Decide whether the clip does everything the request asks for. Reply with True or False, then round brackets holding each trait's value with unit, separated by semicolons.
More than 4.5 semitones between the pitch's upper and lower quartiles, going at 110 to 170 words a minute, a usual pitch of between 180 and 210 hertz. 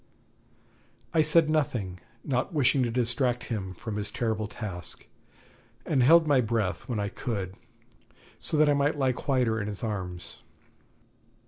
False (5.2 semitones; 145 wpm; 120 Hz)